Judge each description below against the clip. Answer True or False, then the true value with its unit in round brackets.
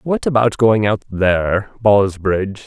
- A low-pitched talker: True (105 Hz)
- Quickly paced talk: False (135 wpm)